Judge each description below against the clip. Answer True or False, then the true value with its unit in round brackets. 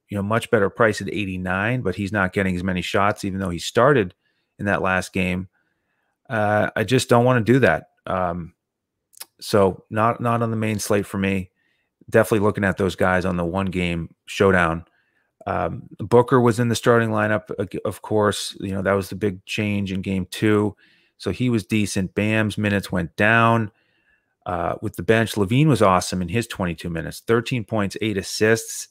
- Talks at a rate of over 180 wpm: True (195 wpm)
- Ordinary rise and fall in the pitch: True (3.1 semitones)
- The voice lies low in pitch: True (100 Hz)